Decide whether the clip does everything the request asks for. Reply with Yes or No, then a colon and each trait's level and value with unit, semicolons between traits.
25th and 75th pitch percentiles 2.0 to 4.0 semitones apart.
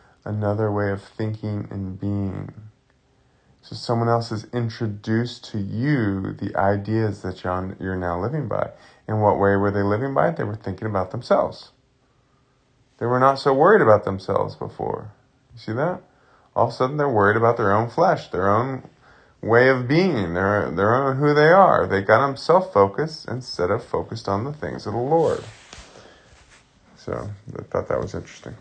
No: average, 4.6 semitones